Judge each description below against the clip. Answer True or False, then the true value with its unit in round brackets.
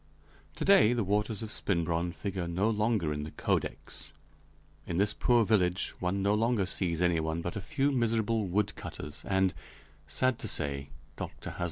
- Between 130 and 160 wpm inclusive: False (175 wpm)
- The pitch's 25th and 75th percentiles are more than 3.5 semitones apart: True (4.4 semitones)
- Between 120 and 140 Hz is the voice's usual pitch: False (100 Hz)